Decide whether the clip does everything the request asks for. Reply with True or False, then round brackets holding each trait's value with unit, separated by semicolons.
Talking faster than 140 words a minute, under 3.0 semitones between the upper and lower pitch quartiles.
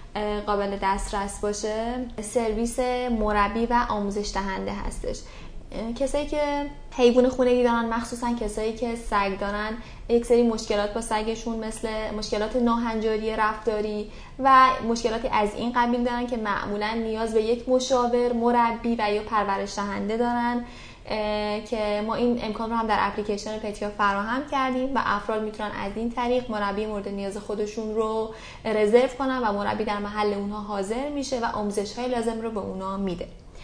True (150 wpm; 2.4 semitones)